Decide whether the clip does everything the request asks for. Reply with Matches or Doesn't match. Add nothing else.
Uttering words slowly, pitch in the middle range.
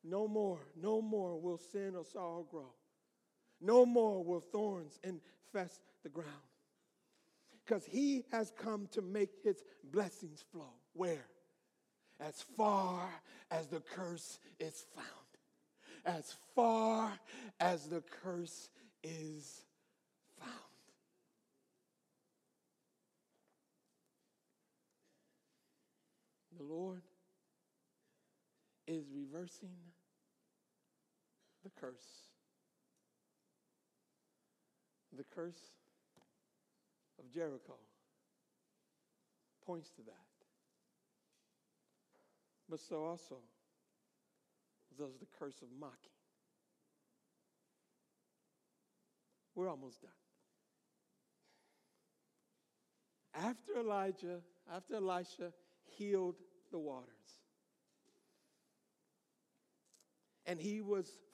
Matches